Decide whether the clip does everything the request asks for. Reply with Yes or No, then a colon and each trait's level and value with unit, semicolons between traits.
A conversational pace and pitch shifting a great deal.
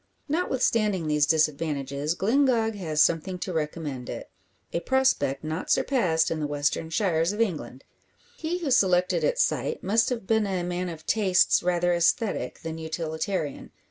Yes: average, 150 wpm; wide, 5.7 semitones